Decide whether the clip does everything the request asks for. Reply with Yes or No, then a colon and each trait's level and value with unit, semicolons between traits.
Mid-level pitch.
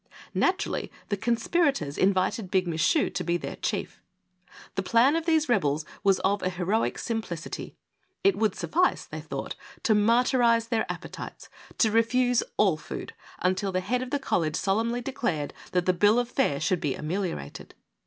No: high, 210 Hz